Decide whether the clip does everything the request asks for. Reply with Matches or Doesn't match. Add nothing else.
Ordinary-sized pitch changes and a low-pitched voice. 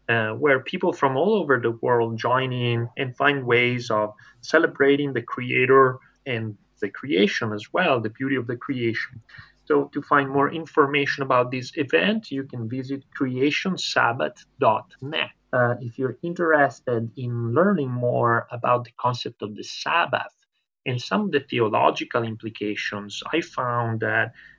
Matches